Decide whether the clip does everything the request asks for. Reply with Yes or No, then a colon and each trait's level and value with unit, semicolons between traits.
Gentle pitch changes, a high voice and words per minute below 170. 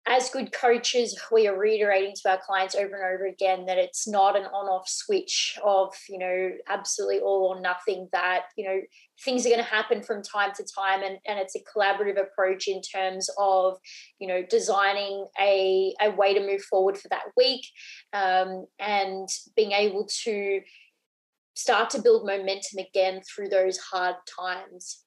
No: narrow, 1.8 semitones; high, 195 Hz; average, 175 wpm